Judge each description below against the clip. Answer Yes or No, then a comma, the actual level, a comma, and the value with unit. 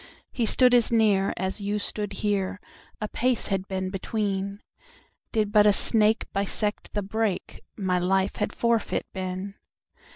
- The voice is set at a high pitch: Yes, high, 205 Hz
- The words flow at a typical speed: No, slow, 130 wpm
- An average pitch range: No, narrow, 2.3 semitones